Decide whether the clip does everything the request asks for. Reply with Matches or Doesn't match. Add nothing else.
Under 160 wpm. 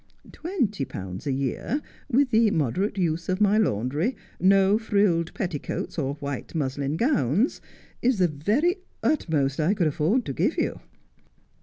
Matches